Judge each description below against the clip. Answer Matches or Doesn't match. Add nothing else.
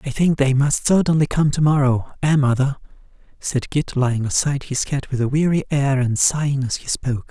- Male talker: Matches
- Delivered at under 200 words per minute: Doesn't match